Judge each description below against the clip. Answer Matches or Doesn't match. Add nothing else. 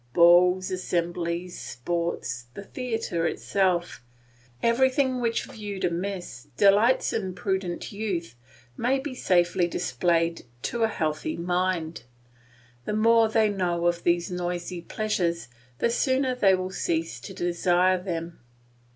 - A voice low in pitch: Doesn't match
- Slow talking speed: Matches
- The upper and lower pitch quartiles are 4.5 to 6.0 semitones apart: Doesn't match